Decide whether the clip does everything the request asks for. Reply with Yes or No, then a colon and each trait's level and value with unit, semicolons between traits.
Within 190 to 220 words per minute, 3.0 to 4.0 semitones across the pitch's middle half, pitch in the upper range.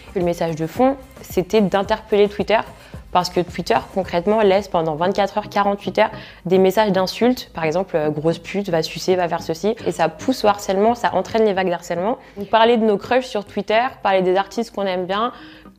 Yes: average, 200 wpm; average, 3.3 semitones; high, 195 Hz